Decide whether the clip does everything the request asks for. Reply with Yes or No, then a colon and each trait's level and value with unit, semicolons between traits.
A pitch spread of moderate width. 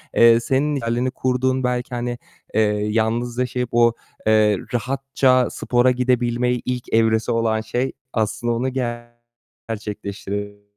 No: narrow, 2.2 semitones